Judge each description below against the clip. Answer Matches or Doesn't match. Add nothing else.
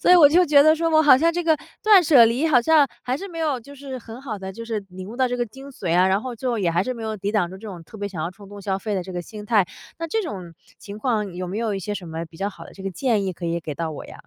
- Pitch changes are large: Matches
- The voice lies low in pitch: Doesn't match